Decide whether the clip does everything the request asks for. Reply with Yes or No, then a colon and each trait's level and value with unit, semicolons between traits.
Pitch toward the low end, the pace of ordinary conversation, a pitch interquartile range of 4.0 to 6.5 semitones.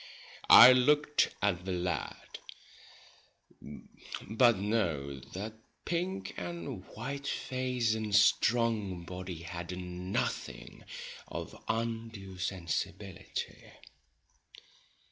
No: low, 100 Hz; slow, 80 wpm; average, 4.6 semitones